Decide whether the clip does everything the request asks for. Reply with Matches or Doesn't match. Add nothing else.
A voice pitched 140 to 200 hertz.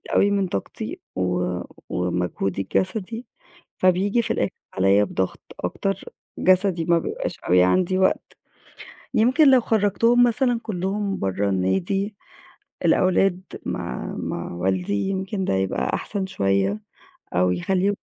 Matches